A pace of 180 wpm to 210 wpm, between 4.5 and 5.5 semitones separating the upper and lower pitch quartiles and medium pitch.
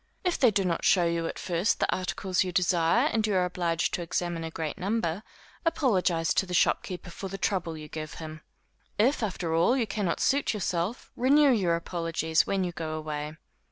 No: average, 195 wpm; average, 3.8 semitones; medium, 180 Hz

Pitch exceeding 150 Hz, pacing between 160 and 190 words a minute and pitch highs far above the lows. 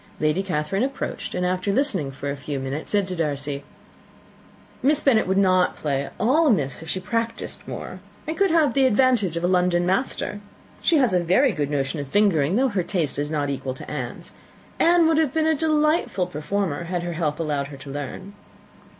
No: medium, 185 Hz; average, 200 wpm; wide, 8.8 semitones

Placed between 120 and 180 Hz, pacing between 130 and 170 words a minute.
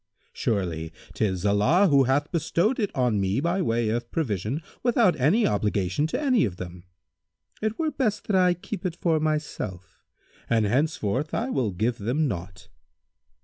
Yes: low, 135 Hz; average, 160 wpm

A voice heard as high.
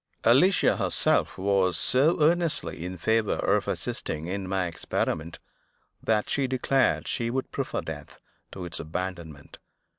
No: very low, 95 Hz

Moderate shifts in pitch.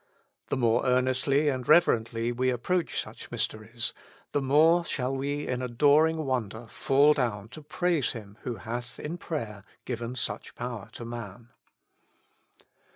Yes: average, 3.7 semitones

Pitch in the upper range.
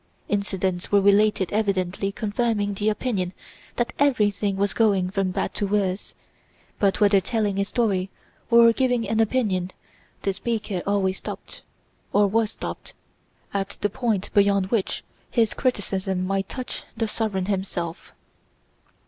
Yes: high, 200 Hz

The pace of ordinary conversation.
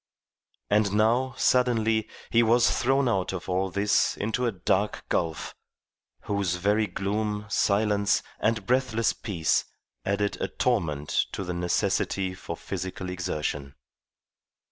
No: slow, 120 wpm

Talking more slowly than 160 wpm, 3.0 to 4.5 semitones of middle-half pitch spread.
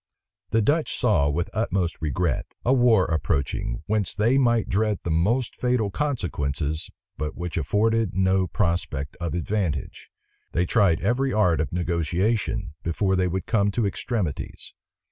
No: average, 145 wpm; average, 4.9 semitones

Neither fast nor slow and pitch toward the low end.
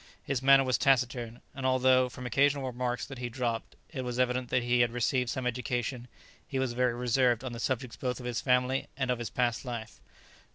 No: fast, 210 wpm; low, 125 Hz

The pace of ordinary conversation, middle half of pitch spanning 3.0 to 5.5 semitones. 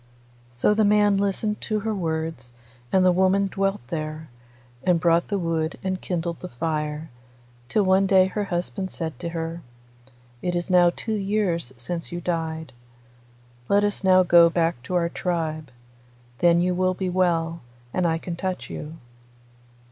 No: average, 165 wpm; narrow, 2.6 semitones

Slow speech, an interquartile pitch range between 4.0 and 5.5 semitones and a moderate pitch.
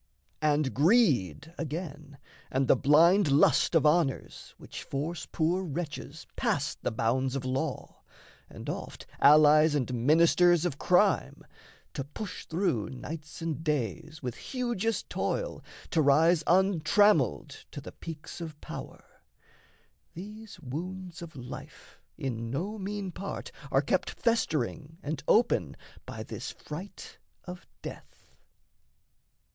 Yes: slow, 120 wpm; average, 4.4 semitones; medium, 160 Hz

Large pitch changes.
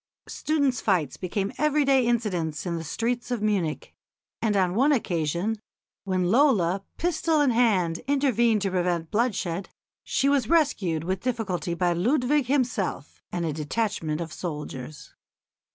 Yes: wide, 6.4 semitones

